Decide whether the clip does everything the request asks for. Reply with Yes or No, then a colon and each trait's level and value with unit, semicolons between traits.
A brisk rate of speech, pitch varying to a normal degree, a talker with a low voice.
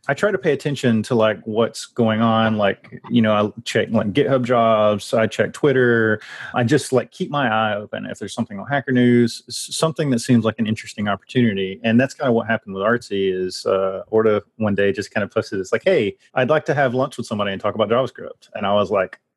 Yes: fast, 235 wpm; average, 3.2 semitones; low, 115 Hz